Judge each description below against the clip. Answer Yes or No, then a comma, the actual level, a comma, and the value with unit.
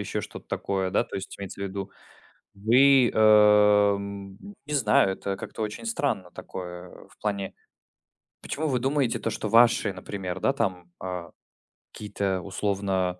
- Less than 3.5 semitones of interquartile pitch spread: Yes, average, 2.7 semitones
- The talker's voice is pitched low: Yes, low, 100 Hz